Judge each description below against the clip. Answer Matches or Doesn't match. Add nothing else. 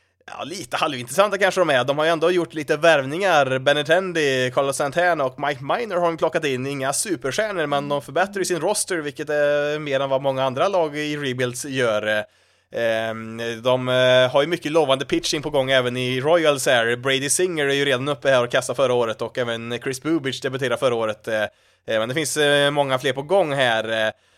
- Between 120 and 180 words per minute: Doesn't match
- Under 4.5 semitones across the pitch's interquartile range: Matches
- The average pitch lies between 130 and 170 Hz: Matches